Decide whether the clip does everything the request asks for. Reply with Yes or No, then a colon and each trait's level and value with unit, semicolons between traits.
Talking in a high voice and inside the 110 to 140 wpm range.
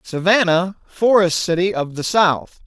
No: medium, 180 Hz; slow, 135 wpm